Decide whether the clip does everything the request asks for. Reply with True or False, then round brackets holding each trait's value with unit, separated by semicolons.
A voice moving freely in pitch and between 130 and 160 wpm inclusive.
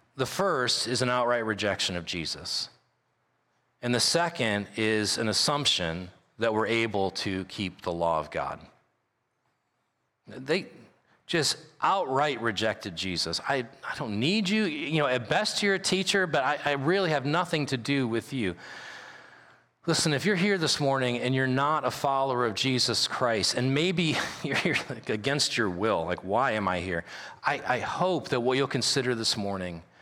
False (5.7 semitones; 170 wpm)